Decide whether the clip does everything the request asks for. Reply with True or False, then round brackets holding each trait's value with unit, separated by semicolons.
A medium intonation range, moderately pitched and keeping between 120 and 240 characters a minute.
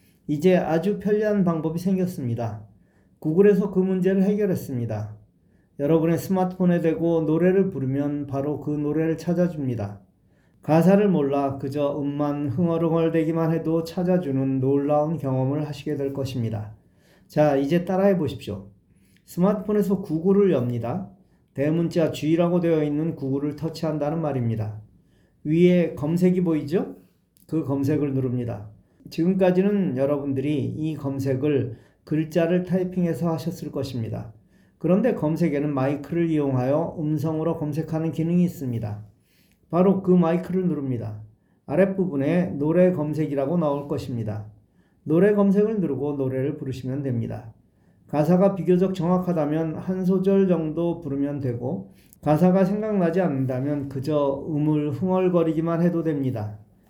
False (4.4 semitones; 155 Hz; 325 characters per minute)